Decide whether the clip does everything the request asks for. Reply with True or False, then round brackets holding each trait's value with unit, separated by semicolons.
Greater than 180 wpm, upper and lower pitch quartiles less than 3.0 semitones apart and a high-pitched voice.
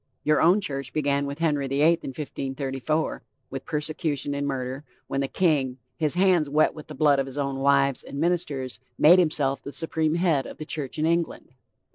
False (195 wpm; 2.6 semitones; 145 Hz)